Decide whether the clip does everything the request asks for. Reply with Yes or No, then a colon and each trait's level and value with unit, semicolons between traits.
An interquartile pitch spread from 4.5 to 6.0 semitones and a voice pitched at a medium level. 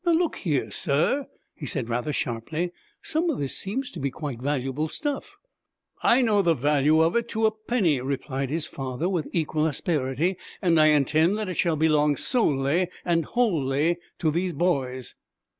Yes: average, 5.2 semitones; medium, 160 Hz